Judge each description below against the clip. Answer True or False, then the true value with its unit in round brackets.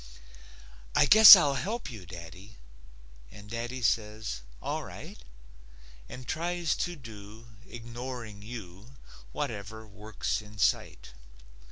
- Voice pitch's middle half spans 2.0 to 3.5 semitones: False (3.9 semitones)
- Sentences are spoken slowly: True (110 wpm)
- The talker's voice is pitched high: False (110 Hz)